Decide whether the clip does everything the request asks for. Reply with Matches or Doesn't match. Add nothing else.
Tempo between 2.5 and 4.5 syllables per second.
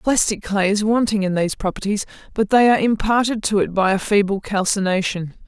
Doesn't match